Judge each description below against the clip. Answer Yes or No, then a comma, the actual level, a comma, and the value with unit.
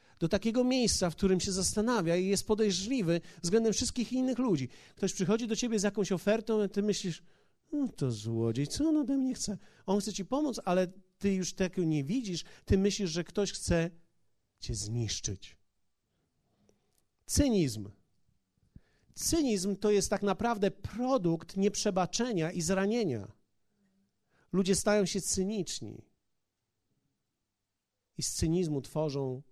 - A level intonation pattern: No, average, 4.3 semitones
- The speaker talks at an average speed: Yes, average, 135 wpm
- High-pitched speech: Yes, high, 195 Hz